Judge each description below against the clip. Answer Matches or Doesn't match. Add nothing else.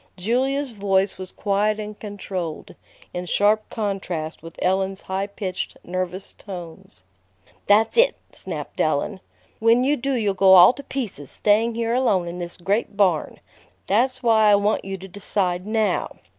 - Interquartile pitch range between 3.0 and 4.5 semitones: Matches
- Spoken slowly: Doesn't match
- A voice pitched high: Matches